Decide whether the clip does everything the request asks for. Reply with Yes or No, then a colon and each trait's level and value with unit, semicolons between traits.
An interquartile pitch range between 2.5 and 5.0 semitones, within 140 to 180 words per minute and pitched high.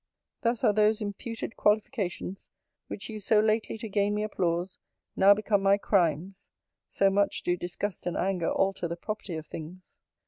Yes: average, 2.9 semitones; average, 165 wpm; high, 200 Hz